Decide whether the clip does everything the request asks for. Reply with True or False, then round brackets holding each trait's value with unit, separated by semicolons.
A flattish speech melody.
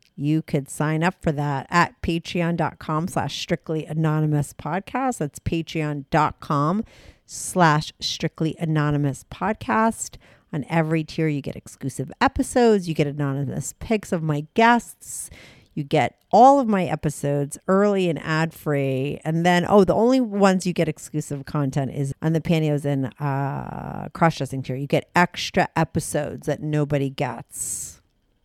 False (3.6 semitones)